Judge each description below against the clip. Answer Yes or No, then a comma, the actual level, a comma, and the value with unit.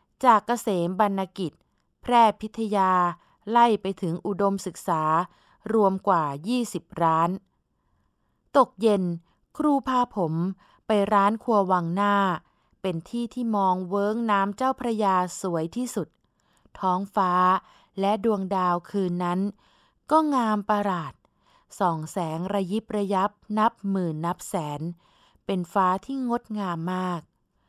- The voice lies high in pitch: Yes, high, 195 Hz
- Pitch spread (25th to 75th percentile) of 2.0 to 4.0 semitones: Yes, average, 3.2 semitones